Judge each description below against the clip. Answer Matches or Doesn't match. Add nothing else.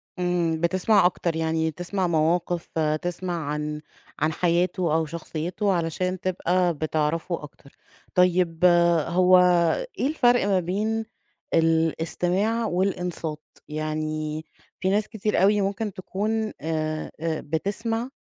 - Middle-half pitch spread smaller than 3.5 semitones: Matches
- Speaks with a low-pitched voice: Doesn't match